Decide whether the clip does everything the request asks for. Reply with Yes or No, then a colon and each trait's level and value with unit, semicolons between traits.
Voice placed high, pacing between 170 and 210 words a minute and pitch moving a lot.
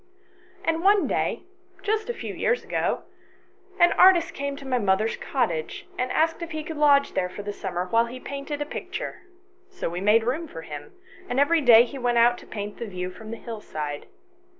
Yes: high, 245 Hz; average, 200 wpm; wide, 7.1 semitones